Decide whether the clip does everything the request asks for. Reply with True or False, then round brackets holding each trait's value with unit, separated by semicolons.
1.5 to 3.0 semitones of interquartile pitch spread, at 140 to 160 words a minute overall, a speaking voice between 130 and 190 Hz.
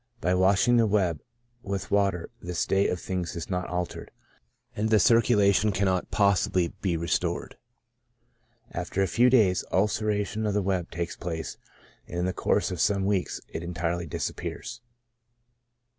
False (2.7 semitones; 150 wpm; 95 Hz)